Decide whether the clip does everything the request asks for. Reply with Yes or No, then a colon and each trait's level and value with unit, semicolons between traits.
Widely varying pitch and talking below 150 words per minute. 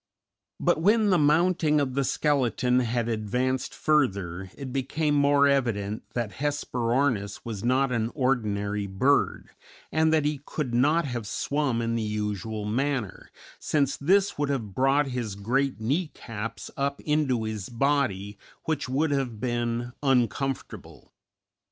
No: average, 4.3 semitones; average, 140 wpm